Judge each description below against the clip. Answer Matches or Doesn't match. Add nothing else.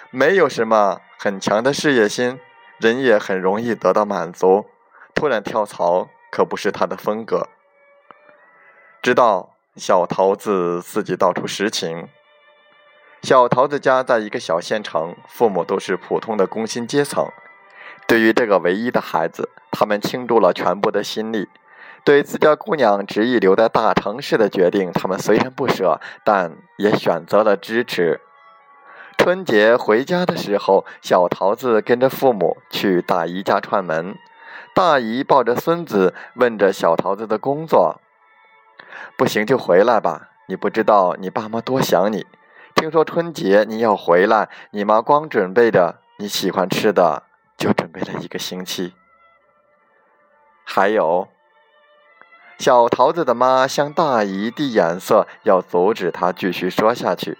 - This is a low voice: Matches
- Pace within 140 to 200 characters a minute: Doesn't match